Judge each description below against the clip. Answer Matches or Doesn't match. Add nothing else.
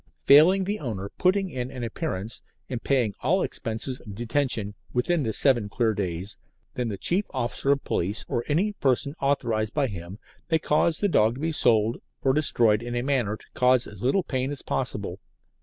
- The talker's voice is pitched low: Matches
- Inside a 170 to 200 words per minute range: Matches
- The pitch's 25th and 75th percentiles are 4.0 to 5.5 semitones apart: Matches